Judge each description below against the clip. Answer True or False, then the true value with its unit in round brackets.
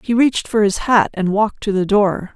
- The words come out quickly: True (255 wpm)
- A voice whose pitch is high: True (210 Hz)